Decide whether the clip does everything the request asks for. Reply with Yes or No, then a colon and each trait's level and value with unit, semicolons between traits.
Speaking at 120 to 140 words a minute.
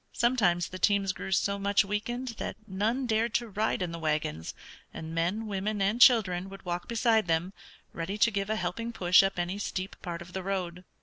No: average, 200 wpm